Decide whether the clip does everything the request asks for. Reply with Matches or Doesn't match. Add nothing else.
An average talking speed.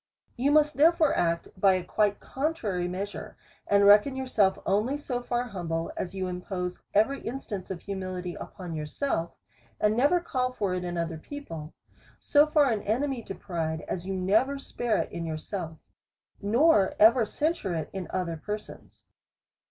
Matches